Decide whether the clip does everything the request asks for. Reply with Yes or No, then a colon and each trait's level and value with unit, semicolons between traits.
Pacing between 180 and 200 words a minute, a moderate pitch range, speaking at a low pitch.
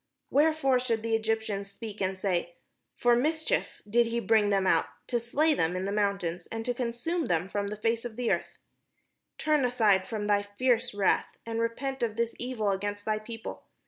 No: average, 190 wpm; average, 3.2 semitones; high, 225 Hz